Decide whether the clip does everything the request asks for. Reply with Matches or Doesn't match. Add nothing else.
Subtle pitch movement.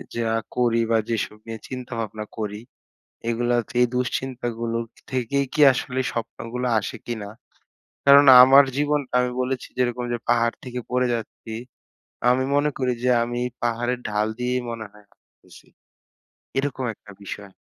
Matches